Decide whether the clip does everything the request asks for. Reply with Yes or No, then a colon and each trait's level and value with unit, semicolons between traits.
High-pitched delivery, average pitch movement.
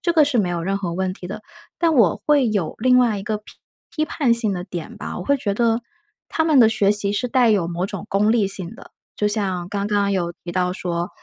Yes: high, 205 Hz; average, 4.4 semitones